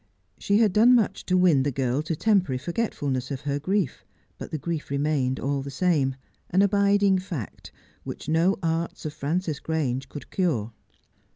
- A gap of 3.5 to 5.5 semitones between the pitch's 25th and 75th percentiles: Yes, average, 5.2 semitones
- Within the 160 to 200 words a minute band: Yes, average, 170 wpm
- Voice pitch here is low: No, medium, 160 Hz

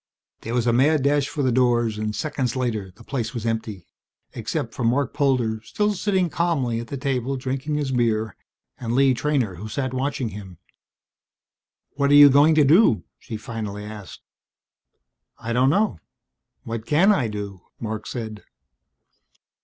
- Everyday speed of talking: Yes, average, 160 wpm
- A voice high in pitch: No, low, 125 Hz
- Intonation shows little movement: No, average, 4.2 semitones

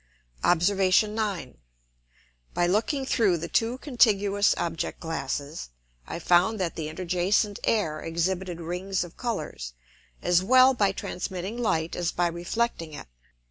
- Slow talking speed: Yes, slow, 130 wpm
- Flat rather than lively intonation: No, average, 3.9 semitones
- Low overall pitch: No, medium, 180 Hz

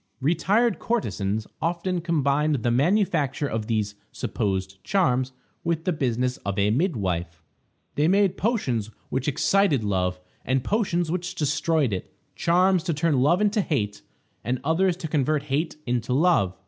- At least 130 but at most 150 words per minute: Yes, average, 145 wpm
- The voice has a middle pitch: Yes, medium, 145 Hz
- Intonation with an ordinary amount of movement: No, wide, 7.4 semitones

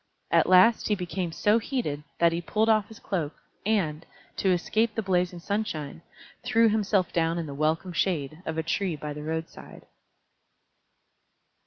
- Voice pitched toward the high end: No, medium, 180 Hz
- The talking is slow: No, average, 160 wpm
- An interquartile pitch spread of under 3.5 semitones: No, average, 4.6 semitones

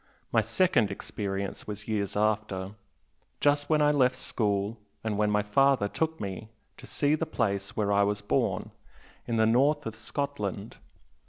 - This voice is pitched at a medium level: No, low, 110 Hz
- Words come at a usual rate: Yes, average, 160 wpm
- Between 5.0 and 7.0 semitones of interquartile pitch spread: Yes, average, 5.3 semitones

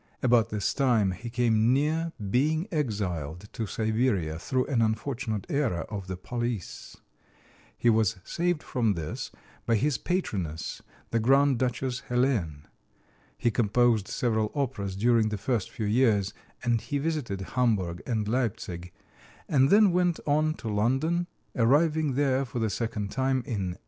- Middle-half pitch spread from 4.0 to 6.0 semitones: Yes, average, 4.6 semitones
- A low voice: Yes, low, 120 Hz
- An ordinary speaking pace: Yes, average, 145 wpm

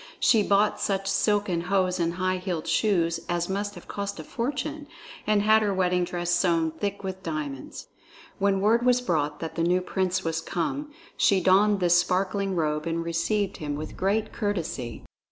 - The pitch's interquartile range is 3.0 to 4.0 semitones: Yes, average, 3.3 semitones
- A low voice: No, medium, 185 Hz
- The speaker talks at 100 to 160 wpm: No, average, 175 wpm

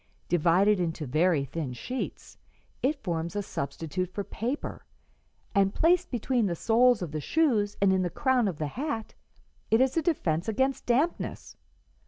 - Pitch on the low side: No, high, 205 Hz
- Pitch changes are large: Yes, wide, 7.3 semitones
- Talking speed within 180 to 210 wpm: No, average, 160 wpm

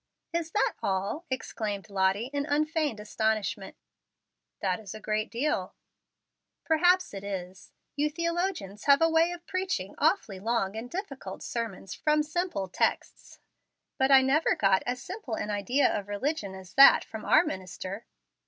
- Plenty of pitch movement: Yes, wide, 7.6 semitones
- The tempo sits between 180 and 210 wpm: No, average, 150 wpm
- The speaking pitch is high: Yes, high, 235 Hz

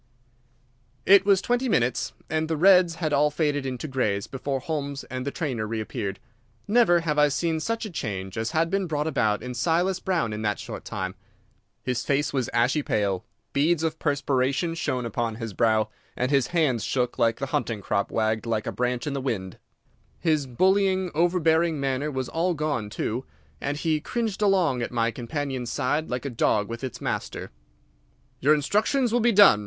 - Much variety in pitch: Yes, wide, 5.8 semitones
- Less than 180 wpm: No, average, 185 wpm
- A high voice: No, medium, 140 Hz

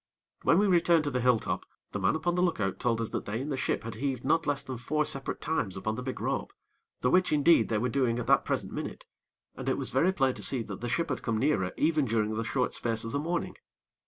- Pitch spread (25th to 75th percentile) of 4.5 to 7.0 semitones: Yes, average, 5.1 semitones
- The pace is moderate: No, fast, 270 wpm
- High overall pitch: No, low, 130 Hz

